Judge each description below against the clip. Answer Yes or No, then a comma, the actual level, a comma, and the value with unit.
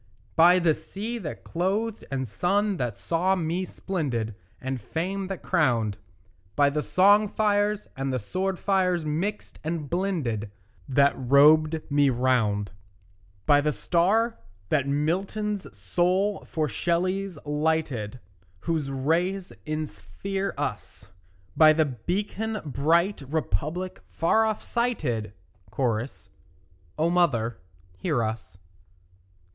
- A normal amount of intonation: No, wide, 6.1 semitones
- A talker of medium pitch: Yes, medium, 160 Hz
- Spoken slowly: Yes, slow, 115 wpm